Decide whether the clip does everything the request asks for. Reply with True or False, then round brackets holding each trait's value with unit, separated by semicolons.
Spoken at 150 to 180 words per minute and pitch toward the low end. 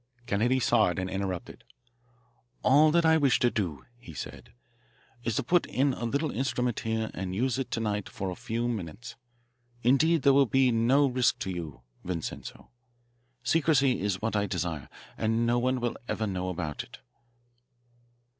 True (170 wpm; 115 Hz)